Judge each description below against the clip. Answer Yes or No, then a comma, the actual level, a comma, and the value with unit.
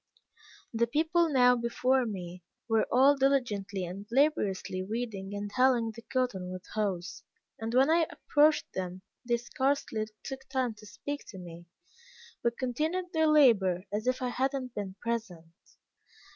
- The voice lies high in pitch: Yes, high, 235 Hz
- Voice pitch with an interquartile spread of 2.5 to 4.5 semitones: No, average, 5.2 semitones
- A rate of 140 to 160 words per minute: Yes, average, 150 wpm